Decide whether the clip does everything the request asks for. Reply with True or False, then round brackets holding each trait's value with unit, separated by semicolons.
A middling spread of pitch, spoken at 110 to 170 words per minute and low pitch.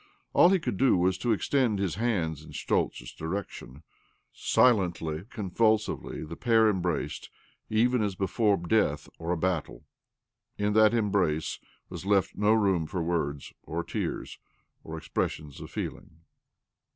True (5.0 semitones; 140 wpm; 95 Hz)